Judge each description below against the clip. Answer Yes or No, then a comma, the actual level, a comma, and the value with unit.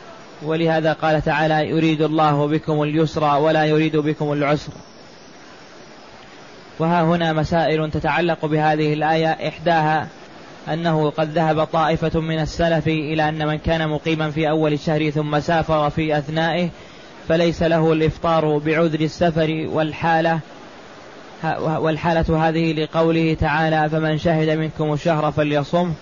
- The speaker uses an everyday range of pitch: No, narrow, 1.0 semitones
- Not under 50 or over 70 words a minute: No, average, 120 wpm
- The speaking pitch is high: No, medium, 155 Hz